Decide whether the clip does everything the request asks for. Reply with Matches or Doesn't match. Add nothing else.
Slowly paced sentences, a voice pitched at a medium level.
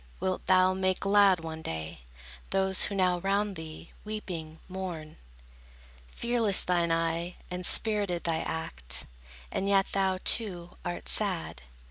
Matches